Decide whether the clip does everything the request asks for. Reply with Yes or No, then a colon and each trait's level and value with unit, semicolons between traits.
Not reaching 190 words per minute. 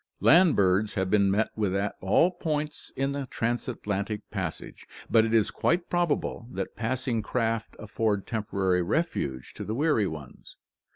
Yes: average, 155 wpm